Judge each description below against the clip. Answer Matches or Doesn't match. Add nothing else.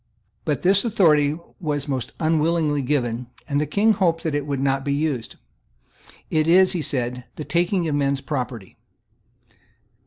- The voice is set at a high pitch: Doesn't match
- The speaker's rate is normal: Matches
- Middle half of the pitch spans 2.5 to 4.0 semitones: Matches